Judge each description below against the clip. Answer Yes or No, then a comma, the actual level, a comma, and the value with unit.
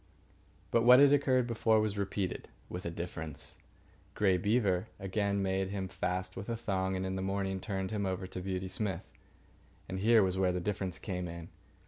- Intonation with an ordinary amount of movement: No, narrow, 2.1 semitones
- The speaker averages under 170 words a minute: No, average, 180 wpm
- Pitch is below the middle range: Yes, very low, 95 Hz